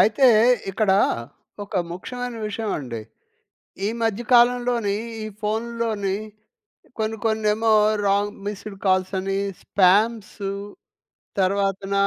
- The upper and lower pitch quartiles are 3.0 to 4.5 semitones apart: No, narrow, 2.5 semitones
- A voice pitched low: No, high, 210 Hz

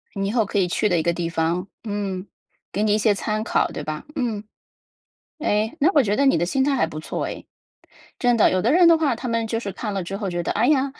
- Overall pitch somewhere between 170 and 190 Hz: No, high, 210 Hz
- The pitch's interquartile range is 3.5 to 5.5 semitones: Yes, average, 4.9 semitones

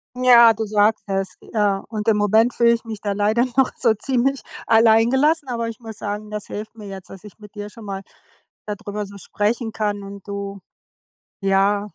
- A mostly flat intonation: Yes, narrow, 2.2 semitones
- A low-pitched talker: No, high, 215 Hz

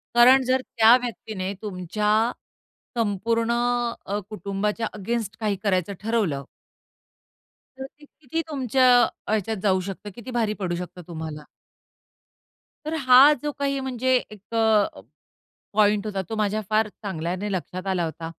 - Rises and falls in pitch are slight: No, average, 3.7 semitones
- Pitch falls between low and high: No, high, 210 Hz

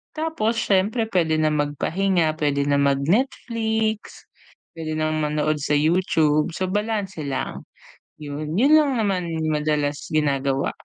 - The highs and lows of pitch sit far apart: Yes, wide, 5.8 semitones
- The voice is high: No, medium, 155 Hz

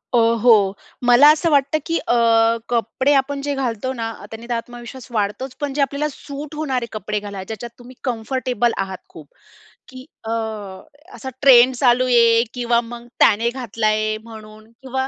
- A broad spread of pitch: No, average, 3.0 semitones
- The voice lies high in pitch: Yes, high, 240 Hz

